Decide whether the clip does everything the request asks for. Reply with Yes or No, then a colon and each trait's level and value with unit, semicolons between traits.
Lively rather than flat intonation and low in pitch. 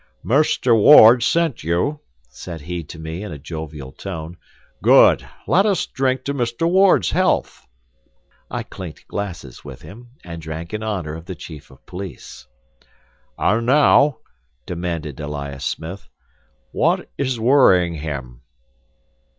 Yes: wide, 7.6 semitones; very low, 90 Hz